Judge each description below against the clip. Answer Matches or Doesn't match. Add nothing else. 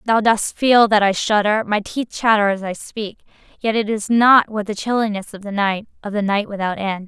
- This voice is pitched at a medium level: Doesn't match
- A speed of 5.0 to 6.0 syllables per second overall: Matches